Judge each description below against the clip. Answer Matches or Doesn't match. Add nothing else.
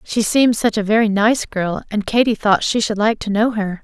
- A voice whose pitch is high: Matches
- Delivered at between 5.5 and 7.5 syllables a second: Doesn't match